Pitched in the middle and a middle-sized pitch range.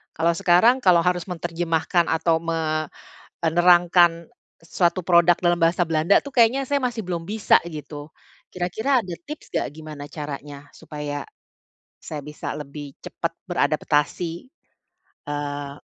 Yes: medium, 170 Hz; average, 3.0 semitones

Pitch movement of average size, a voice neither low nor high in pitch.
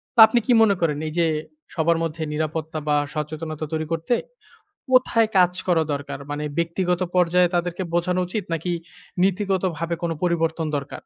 No: narrow, 2.3 semitones; medium, 170 Hz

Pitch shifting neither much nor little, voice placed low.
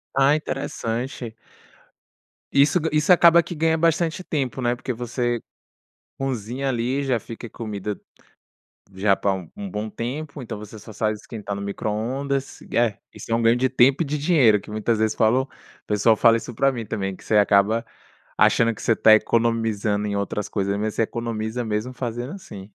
Yes: average, 4.1 semitones; low, 115 Hz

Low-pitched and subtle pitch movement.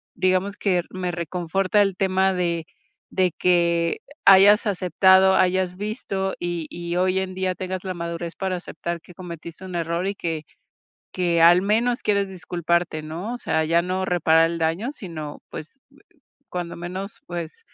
No: medium, 180 Hz; narrow, 2.0 semitones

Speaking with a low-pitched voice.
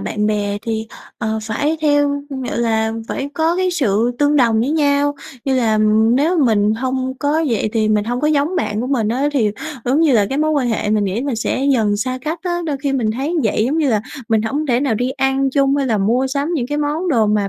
No: very high, 260 Hz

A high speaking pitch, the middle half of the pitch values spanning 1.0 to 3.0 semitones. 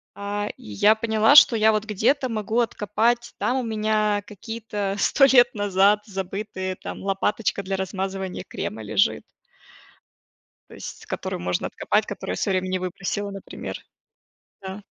Yes: high, 205 Hz; narrow, 2.4 semitones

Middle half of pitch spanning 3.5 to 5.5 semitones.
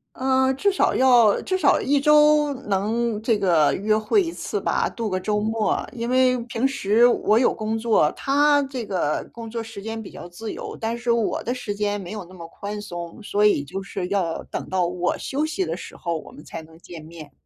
Yes: average, 5.0 semitones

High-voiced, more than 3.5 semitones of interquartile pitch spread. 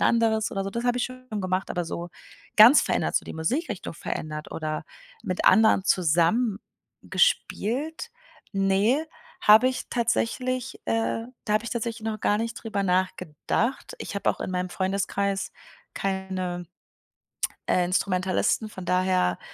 Yes: high, 200 Hz; average, 4.1 semitones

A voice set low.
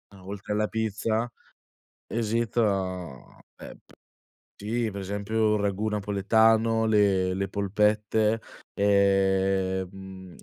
Yes: low, 100 Hz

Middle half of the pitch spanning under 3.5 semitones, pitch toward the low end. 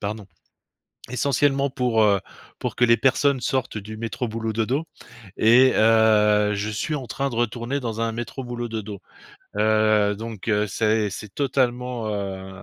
Yes: average, 2.9 semitones; low, 115 Hz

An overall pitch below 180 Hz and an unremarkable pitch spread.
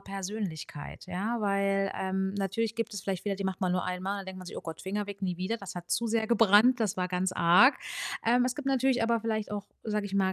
No: high, 200 Hz; average, 3.0 semitones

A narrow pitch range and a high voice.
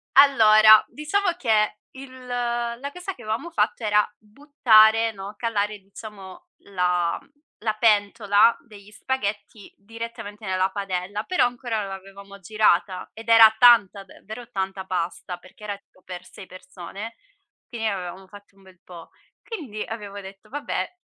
No: average, 3.0 semitones; high, 210 Hz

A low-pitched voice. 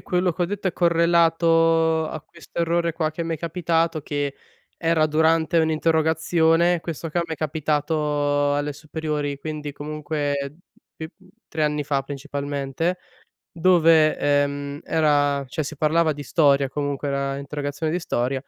No: medium, 155 Hz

